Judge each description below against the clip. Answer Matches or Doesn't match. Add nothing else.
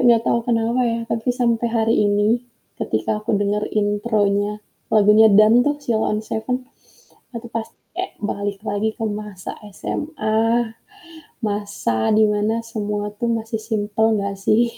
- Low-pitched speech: Doesn't match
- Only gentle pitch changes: Matches